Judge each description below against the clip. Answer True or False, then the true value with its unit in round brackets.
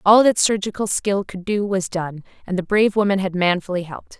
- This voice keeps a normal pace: False (215 wpm)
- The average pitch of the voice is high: True (195 Hz)